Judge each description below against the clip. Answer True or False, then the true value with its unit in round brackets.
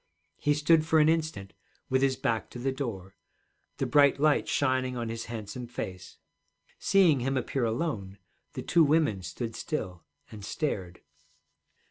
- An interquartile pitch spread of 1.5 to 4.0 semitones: False (5.4 semitones)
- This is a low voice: True (130 Hz)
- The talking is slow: False (150 wpm)